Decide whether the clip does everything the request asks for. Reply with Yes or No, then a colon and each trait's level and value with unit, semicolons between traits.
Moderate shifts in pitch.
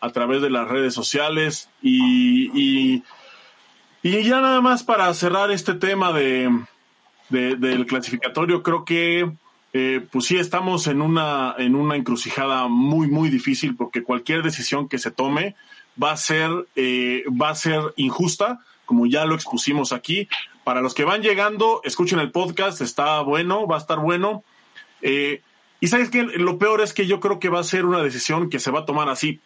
No: wide, 6.8 semitones